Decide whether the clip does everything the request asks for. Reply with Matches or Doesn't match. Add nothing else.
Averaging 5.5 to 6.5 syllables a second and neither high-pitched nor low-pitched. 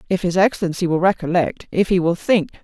Matches